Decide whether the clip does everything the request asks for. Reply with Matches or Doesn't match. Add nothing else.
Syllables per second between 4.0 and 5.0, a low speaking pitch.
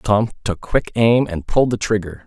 Matches